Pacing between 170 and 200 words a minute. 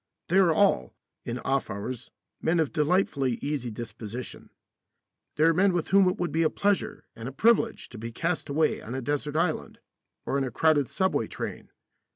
Yes: average, 190 wpm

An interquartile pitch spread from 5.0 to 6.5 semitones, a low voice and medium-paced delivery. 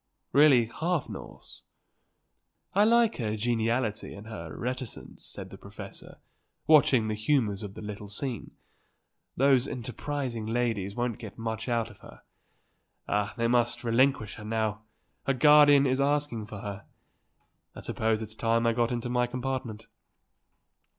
No: average, 3.3 semitones; low, 115 Hz; average, 145 wpm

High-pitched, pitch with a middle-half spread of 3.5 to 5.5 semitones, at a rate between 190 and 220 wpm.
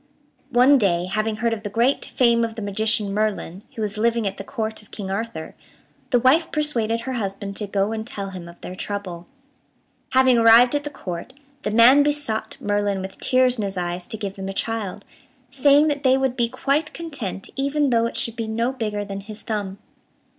Yes: high, 220 Hz; average, 4.2 semitones; fast, 205 wpm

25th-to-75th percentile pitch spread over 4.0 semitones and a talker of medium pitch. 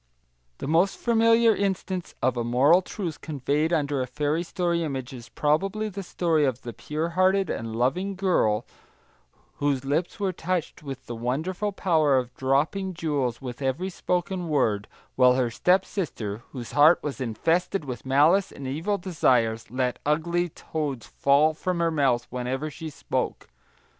Yes: wide, 5.6 semitones; medium, 150 Hz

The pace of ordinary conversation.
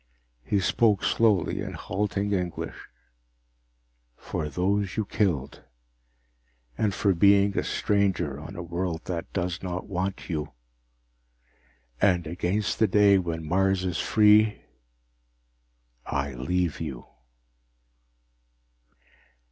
No: slow, 105 wpm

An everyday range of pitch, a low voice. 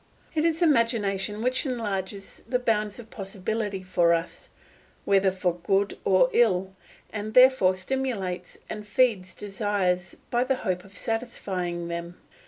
No: average, 3.8 semitones; high, 200 Hz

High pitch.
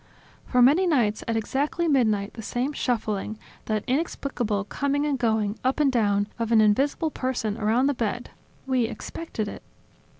Yes: high, 240 Hz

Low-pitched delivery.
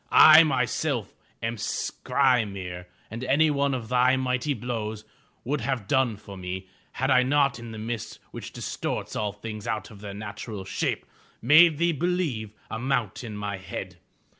Yes: low, 120 Hz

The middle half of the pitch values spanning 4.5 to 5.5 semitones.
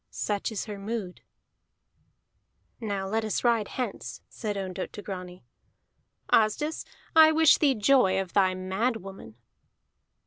No: average, 3.5 semitones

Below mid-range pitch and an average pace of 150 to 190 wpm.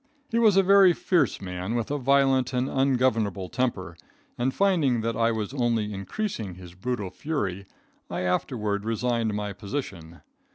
Yes: low, 115 Hz; average, 155 wpm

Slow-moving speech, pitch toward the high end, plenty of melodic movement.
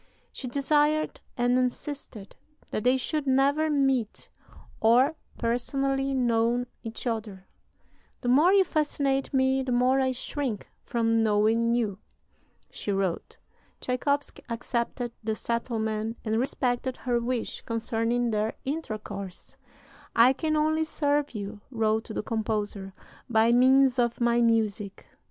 No: slow, 125 wpm; high, 240 Hz; average, 3.3 semitones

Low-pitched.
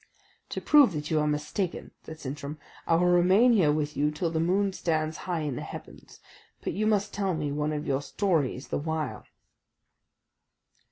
No: medium, 160 Hz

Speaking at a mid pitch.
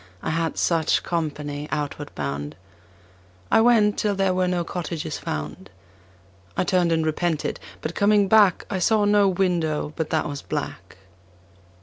Yes: medium, 170 Hz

